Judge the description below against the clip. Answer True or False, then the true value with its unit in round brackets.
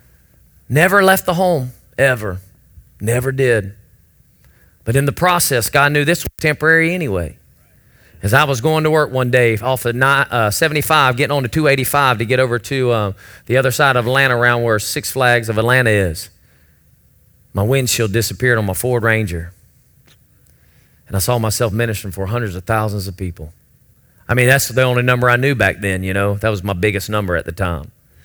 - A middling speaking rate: True (185 wpm)